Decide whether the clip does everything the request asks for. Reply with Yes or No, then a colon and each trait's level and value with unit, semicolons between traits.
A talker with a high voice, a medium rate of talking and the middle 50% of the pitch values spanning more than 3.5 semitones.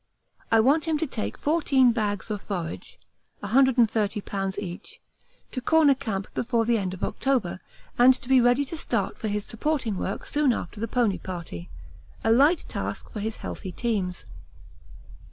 Yes: high, 225 Hz; average, 165 wpm; average, 4.8 semitones